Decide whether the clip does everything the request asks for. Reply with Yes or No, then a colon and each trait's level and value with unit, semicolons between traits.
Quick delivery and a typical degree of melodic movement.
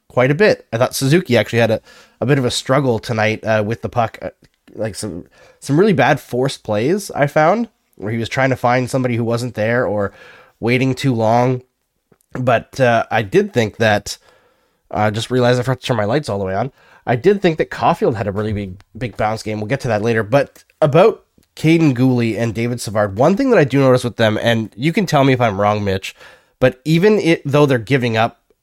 Yes: fast, 235 wpm; average, 3.6 semitones